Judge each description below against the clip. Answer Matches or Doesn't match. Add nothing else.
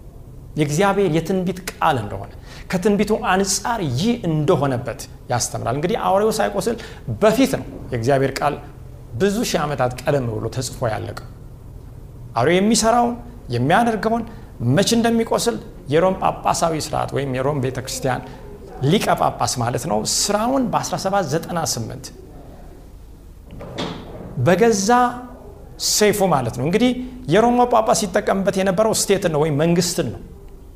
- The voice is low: Doesn't match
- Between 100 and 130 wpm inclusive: Matches